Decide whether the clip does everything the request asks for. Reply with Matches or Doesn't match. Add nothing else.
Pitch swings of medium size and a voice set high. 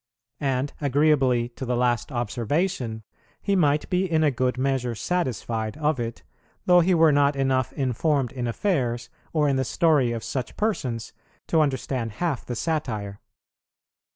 Doesn't match